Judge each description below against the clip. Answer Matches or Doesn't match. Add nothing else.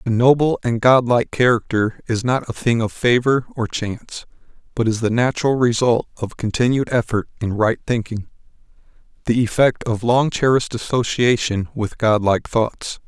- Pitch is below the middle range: Matches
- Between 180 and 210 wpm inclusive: Doesn't match